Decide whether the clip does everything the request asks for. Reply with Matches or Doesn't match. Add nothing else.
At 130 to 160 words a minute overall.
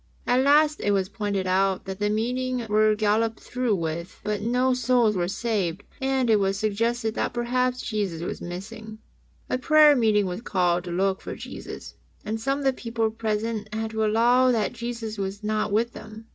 Doesn't match